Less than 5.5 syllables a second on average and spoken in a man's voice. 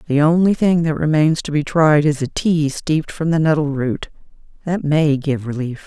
No: 4.9 syllables/s; female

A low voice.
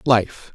Yes: low, 120 Hz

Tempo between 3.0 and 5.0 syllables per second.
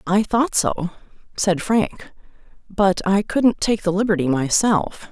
Yes: 3.8 syllables/s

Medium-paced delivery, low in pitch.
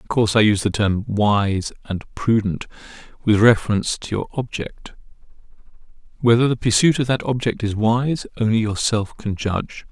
Yes: average, 155 wpm; low, 110 Hz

